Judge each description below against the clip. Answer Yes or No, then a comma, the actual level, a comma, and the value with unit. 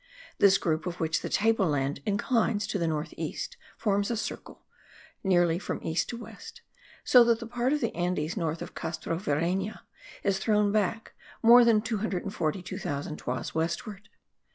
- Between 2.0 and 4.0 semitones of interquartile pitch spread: No, average, 4.9 semitones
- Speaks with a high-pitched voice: Yes, high, 195 Hz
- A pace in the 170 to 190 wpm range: No, average, 155 wpm